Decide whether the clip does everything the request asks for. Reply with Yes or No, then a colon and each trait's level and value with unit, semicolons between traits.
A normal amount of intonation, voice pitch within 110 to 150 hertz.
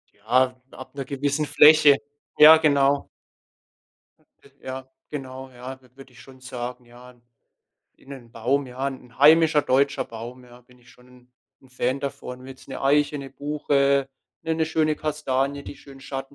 No: narrow, 2.1 semitones; low, 135 Hz